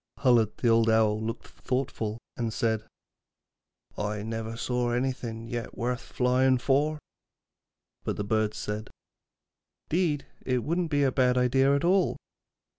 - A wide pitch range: No, average, 3.0 semitones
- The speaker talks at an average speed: No, slow, 130 wpm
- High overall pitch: No, low, 125 Hz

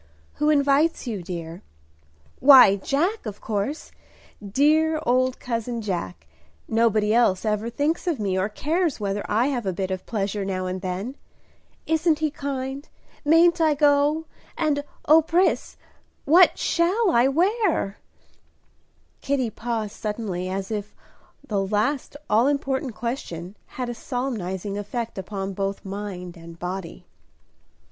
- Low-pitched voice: No, high, 235 Hz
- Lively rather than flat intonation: Yes, wide, 6.7 semitones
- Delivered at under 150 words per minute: Yes, slow, 135 wpm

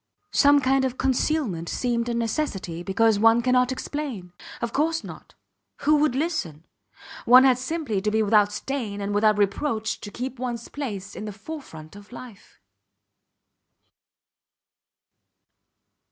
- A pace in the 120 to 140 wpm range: Yes, slow, 135 wpm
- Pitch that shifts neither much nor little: Yes, average, 4.6 semitones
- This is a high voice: Yes, high, 235 Hz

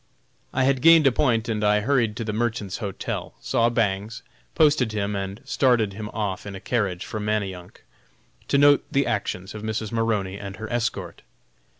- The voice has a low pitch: Yes, low, 110 Hz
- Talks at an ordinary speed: Yes, average, 180 wpm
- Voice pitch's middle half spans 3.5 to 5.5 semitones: No, average, 3.0 semitones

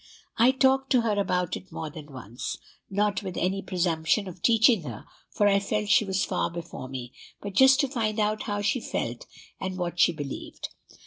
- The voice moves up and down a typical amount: Yes, average, 4.1 semitones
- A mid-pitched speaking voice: No, high, 195 Hz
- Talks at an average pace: Yes, average, 195 wpm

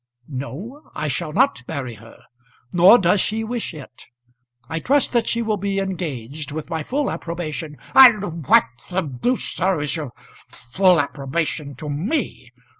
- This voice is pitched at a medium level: Yes, medium, 170 Hz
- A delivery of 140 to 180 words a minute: Yes, average, 160 wpm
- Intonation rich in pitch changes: Yes, wide, 6.2 semitones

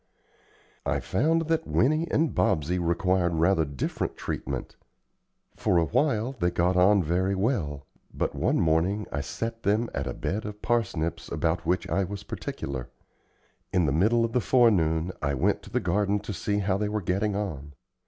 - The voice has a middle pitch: No, very low, 95 Hz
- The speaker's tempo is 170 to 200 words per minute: Yes, average, 175 wpm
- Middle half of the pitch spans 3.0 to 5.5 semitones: Yes, average, 4.7 semitones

